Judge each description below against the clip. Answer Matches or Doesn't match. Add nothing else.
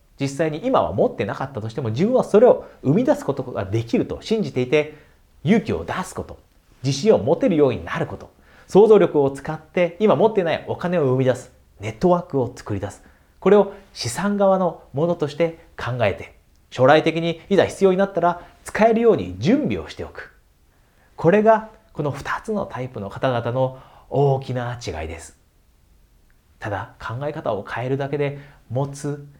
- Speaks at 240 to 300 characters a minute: Doesn't match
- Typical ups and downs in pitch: Doesn't match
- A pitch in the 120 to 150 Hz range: Matches